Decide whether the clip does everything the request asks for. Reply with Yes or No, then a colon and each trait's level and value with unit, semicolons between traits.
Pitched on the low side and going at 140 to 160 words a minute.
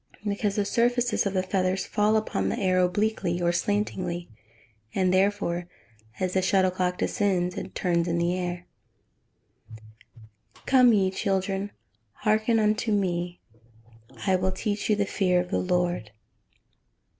No: medium, 185 Hz; average, 145 wpm